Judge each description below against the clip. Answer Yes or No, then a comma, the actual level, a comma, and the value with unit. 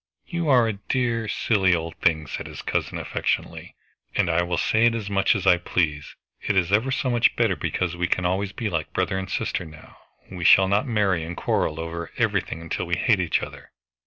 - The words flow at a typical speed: No, fast, 220 wpm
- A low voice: Yes, very low, 95 Hz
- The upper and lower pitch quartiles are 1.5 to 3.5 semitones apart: No, average, 4.4 semitones